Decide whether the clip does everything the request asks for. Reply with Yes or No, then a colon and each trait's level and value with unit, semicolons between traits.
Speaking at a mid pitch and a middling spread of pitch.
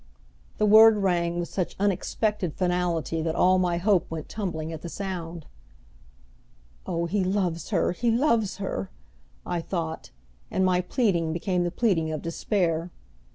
Yes: medium, 180 Hz; average, 3.0 semitones